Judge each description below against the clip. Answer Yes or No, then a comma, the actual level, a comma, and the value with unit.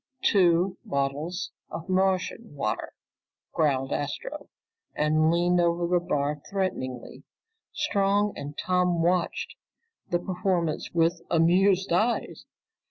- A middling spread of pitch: Yes, average, 3.3 semitones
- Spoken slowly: Yes, slow, 100 wpm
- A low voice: No, medium, 175 Hz